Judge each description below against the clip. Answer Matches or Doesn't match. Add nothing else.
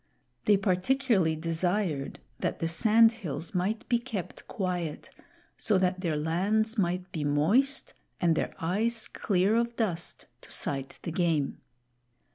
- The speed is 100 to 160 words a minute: Matches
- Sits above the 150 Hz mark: Matches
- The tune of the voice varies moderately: Matches